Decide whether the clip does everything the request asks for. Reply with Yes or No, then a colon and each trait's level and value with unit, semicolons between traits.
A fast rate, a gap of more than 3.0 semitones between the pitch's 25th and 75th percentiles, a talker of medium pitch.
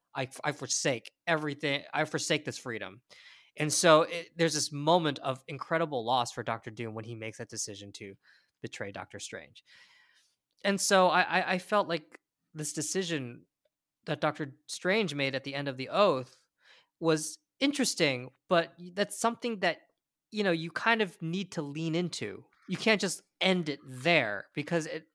No: average, 165 wpm; average, 4.5 semitones; medium, 160 Hz